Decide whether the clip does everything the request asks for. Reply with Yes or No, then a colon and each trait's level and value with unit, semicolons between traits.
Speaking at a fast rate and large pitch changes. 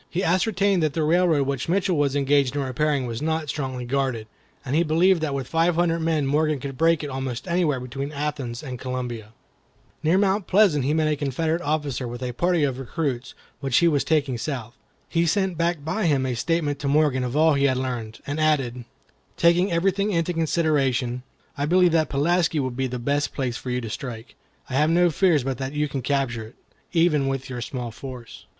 No: fast, 210 wpm; average, 4.1 semitones